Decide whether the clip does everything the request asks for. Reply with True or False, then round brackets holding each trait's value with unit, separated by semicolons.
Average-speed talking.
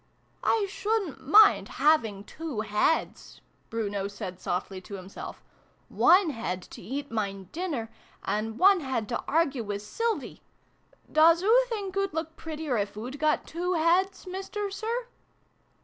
True (150 wpm)